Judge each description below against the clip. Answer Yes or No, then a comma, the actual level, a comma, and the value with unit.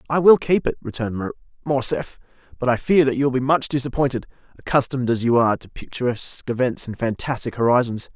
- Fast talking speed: No, average, 185 wpm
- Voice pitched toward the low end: Yes, low, 125 Hz